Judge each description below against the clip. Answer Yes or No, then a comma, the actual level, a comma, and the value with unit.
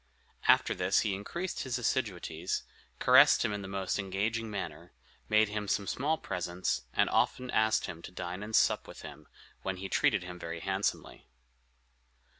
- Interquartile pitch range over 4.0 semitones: No, average, 3.2 semitones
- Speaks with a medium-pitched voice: No, low, 100 Hz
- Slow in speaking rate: No, average, 165 wpm